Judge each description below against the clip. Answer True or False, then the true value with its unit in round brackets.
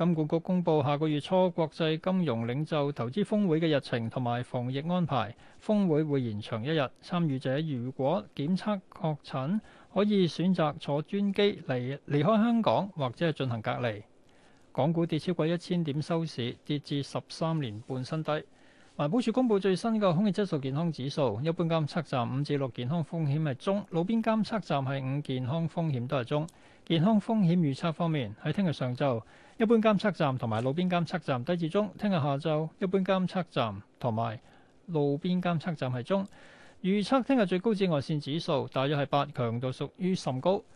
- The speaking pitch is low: False (160 Hz)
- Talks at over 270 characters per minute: True (285 characters per minute)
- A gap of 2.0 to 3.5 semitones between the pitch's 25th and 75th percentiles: False (5.3 semitones)